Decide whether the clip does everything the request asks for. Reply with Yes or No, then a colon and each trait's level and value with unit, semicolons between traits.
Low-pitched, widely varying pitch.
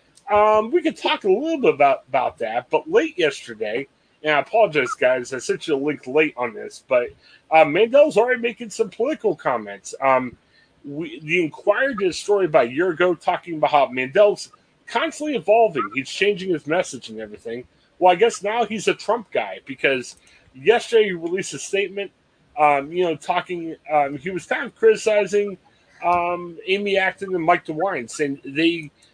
No: medium, 180 Hz; wide, 6.5 semitones